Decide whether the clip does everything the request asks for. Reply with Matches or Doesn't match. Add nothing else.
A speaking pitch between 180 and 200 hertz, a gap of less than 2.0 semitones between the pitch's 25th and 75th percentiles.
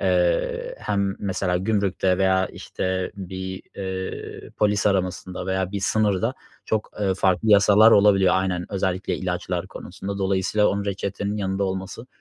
Doesn't match